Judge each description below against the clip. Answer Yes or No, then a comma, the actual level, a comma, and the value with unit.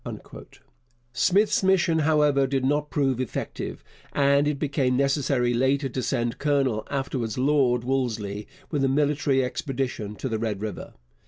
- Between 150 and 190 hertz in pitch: No, low, 135 Hz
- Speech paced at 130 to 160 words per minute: Yes, average, 140 wpm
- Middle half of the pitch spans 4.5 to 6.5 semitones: No, average, 2.9 semitones